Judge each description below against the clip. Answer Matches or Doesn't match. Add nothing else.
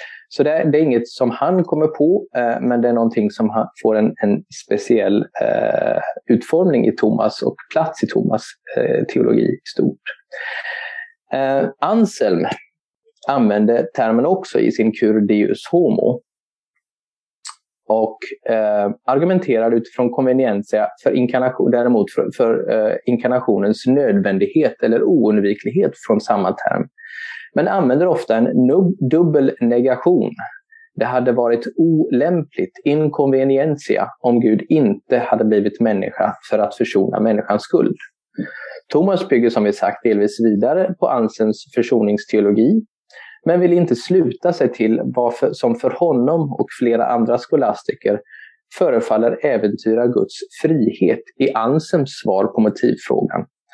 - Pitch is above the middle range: Doesn't match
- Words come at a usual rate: Doesn't match